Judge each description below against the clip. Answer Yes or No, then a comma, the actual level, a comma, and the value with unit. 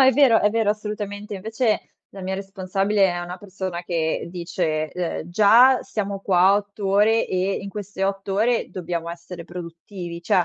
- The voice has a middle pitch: No, high, 195 Hz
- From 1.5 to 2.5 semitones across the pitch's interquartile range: No, average, 2.9 semitones